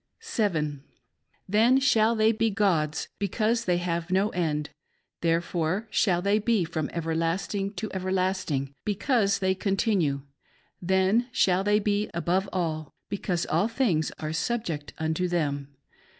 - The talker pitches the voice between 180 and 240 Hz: Yes, high, 190 Hz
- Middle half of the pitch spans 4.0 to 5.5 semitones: Yes, average, 4.3 semitones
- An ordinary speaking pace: No, slow, 125 wpm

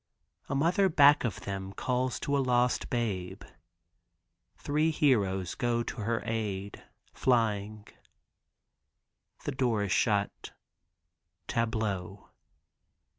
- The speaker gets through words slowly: Yes, slow, 100 wpm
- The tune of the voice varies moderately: Yes, average, 4.4 semitones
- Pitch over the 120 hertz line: No, low, 115 Hz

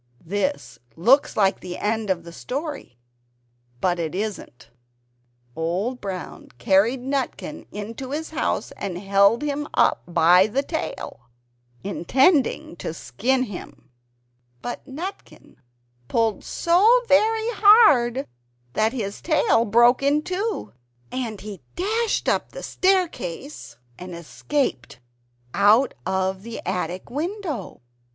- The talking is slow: Yes, slow, 115 wpm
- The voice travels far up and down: Yes, wide, 7.7 semitones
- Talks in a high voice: Yes, high, 235 Hz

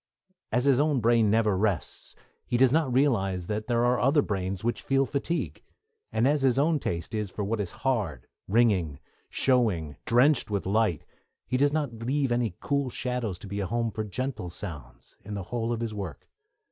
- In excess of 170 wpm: Yes, average, 190 wpm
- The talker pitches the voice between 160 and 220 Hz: No, low, 115 Hz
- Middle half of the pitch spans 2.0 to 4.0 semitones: No, average, 4.8 semitones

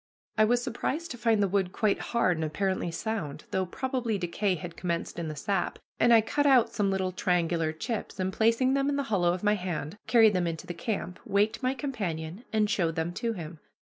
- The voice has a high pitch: Yes, high, 200 Hz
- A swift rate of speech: Yes, fast, 215 wpm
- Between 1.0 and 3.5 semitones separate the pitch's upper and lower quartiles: No, average, 4.7 semitones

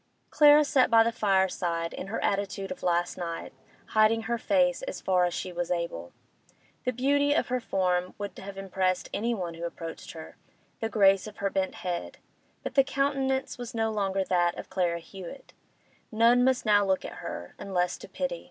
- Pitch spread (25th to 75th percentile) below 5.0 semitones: No, wide, 5.4 semitones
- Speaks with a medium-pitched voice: No, high, 195 Hz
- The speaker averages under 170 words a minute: No, average, 185 wpm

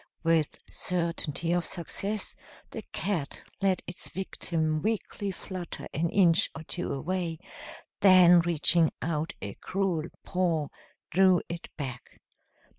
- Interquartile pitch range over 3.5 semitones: No, narrow, 2.5 semitones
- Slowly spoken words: Yes, slow, 115 wpm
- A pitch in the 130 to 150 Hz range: No, medium, 170 Hz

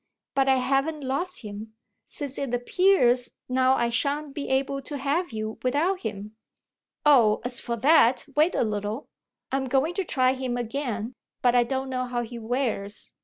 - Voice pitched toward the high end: Yes, very high, 255 Hz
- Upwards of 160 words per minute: Yes, average, 170 wpm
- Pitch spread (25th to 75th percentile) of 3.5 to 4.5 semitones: No, average, 3.0 semitones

